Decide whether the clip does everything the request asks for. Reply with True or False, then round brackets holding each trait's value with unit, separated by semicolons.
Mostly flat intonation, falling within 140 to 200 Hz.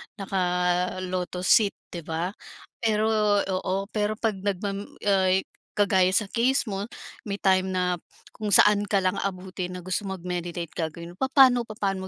True (2.3 semitones; 190 Hz)